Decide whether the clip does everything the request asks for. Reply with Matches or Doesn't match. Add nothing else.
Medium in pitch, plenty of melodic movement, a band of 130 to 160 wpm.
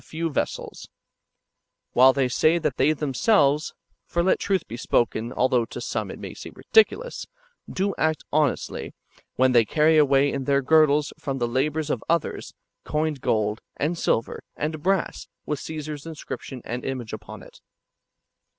Doesn't match